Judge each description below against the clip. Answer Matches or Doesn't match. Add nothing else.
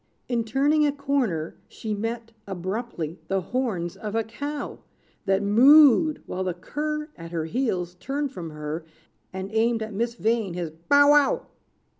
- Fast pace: Doesn't match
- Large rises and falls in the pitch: Matches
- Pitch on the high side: Matches